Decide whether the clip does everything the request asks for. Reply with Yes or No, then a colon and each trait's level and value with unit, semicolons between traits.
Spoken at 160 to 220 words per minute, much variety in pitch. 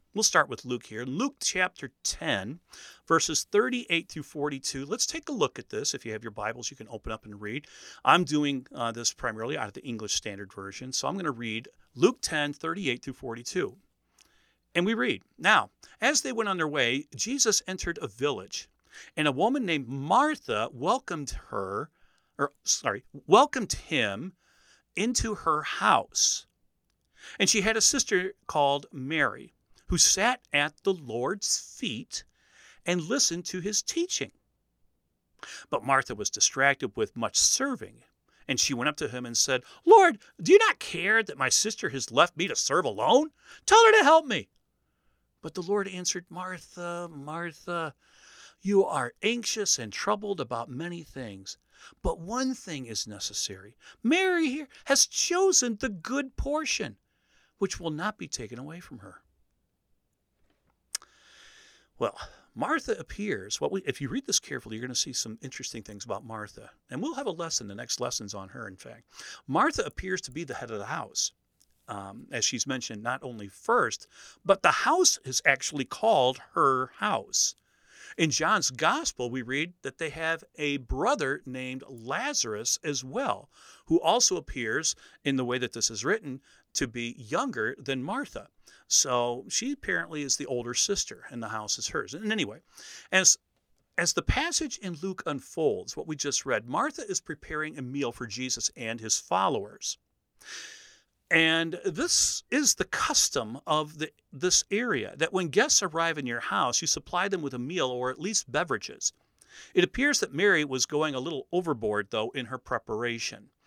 Yes: average, 170 wpm; wide, 8.8 semitones